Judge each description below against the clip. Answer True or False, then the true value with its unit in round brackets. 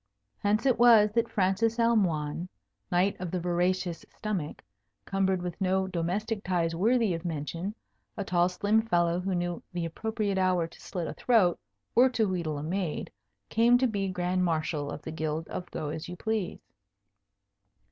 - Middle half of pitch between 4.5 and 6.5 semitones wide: False (3.7 semitones)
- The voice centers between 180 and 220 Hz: True (185 Hz)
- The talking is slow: False (165 wpm)